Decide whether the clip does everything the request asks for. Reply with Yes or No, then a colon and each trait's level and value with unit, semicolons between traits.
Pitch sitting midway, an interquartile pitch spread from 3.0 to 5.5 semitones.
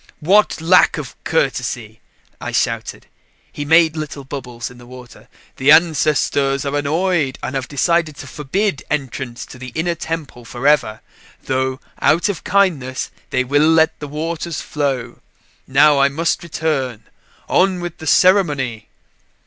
Yes: medium, 145 Hz; average, 3.9 semitones